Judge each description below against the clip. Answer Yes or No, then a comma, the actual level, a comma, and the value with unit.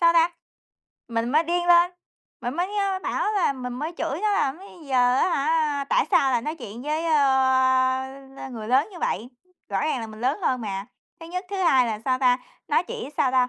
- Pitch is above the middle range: Yes, very high, 270 Hz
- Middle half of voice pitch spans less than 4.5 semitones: No, average, 5.0 semitones